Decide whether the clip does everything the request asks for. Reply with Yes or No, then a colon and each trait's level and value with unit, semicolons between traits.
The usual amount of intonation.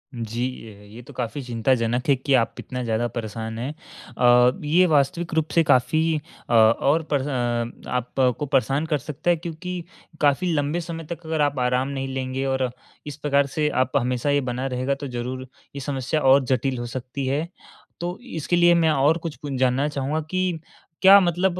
Yes: average, 3.9 semitones